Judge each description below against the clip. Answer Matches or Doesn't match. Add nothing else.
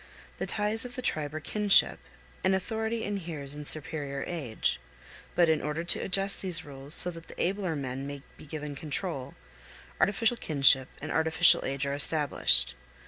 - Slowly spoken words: Doesn't match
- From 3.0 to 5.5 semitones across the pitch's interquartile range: Matches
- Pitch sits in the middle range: Matches